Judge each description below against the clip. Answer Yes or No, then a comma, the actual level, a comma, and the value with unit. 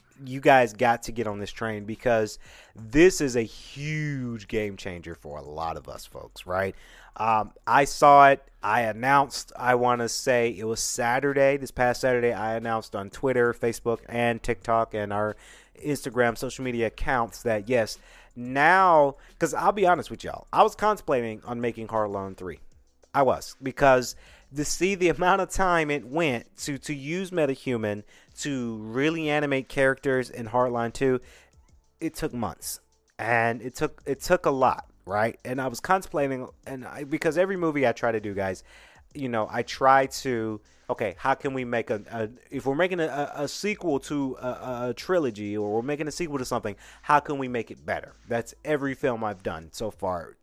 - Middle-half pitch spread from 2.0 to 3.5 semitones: No, average, 4.1 semitones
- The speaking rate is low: No, average, 185 wpm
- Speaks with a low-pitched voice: Yes, low, 125 Hz